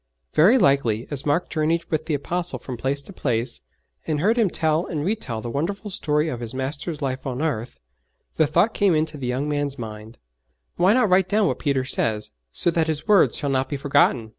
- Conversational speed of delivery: No, fast, 210 wpm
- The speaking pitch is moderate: Yes, medium, 145 Hz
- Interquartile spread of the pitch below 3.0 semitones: No, average, 4.5 semitones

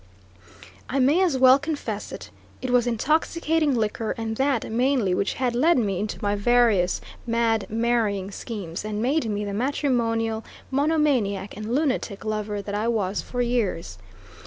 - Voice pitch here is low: No, high, 230 Hz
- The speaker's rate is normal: Yes, average, 155 wpm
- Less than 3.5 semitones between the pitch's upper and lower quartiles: No, average, 4.0 semitones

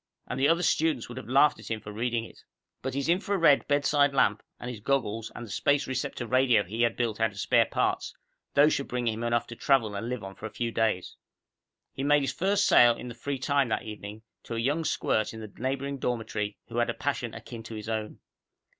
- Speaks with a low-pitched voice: Yes, low, 120 Hz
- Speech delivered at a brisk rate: Yes, fast, 235 wpm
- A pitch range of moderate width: Yes, average, 3.9 semitones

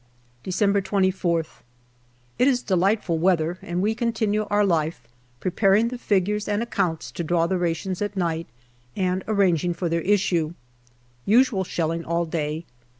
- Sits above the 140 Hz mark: Yes, medium, 185 Hz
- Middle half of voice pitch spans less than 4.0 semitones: Yes, average, 3.6 semitones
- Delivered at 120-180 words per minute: Yes, average, 145 wpm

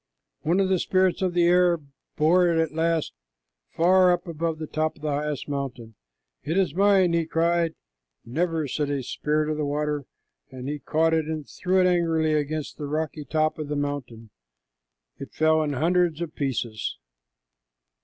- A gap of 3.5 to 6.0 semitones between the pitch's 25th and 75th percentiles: No, average, 2.7 semitones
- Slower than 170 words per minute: No, average, 175 wpm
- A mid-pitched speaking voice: Yes, medium, 155 Hz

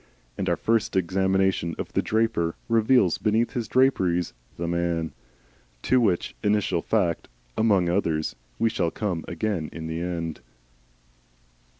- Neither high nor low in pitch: No, very low, 95 Hz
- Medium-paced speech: No, slow, 130 wpm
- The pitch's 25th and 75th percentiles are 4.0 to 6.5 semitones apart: Yes, average, 4.5 semitones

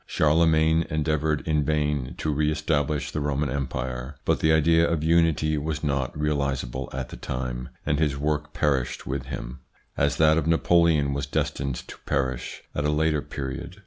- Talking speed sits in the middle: Yes, average, 170 wpm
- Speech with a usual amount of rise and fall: No, narrow, 2.3 semitones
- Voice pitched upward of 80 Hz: No, very low, 75 Hz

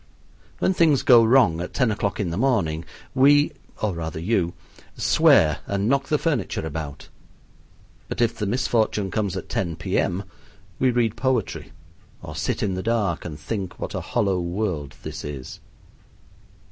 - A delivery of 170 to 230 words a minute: No, average, 160 wpm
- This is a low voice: Yes, low, 100 Hz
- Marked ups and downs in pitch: Yes, wide, 6.2 semitones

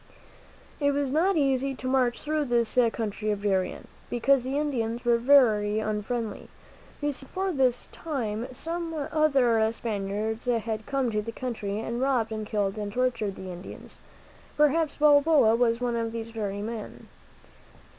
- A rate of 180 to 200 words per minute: No, average, 155 wpm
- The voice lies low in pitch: No, high, 235 Hz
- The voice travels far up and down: No, average, 4.2 semitones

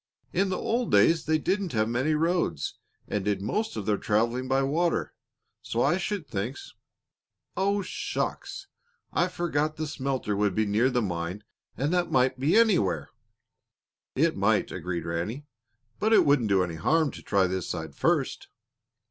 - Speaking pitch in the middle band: No, low, 130 Hz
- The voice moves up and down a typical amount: No, wide, 8.9 semitones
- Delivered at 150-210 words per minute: Yes, average, 165 wpm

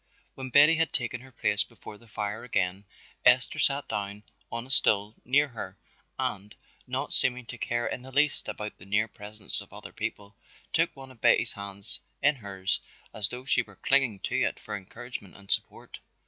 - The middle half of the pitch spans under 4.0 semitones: No, average, 4.3 semitones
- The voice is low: Yes, low, 115 Hz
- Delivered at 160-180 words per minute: No, average, 190 wpm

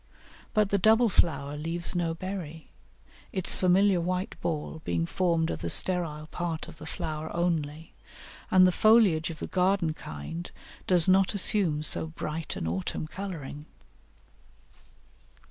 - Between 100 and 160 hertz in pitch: No, medium, 170 Hz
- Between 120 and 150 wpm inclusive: Yes, average, 140 wpm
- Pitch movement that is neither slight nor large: Yes, average, 3.2 semitones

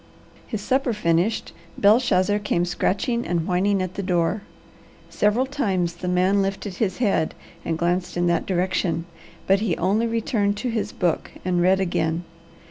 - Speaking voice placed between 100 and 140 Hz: No, high, 190 Hz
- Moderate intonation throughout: Yes, average, 3.0 semitones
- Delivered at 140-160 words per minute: Yes, average, 155 wpm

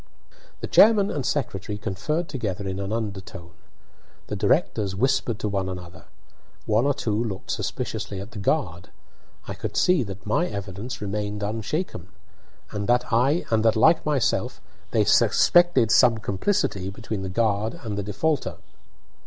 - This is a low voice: Yes, low, 110 Hz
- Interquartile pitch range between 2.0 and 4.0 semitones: No, average, 4.9 semitones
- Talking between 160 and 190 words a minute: No, average, 140 wpm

